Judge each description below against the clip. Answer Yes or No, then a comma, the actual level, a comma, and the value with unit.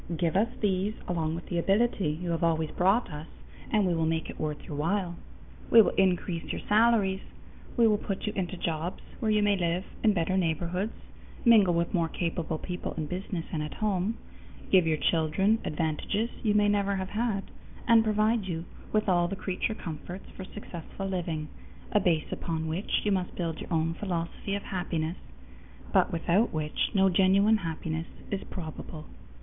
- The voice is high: No, medium, 180 Hz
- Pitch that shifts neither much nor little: Yes, average, 3.7 semitones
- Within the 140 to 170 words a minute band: No, average, 180 wpm